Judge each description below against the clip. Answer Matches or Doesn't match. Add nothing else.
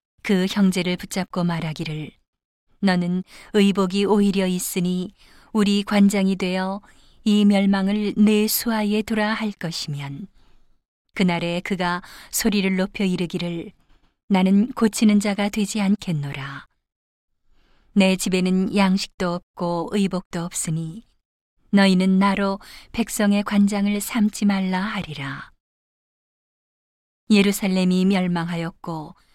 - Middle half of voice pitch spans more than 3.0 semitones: Doesn't match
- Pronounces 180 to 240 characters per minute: Matches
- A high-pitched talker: Matches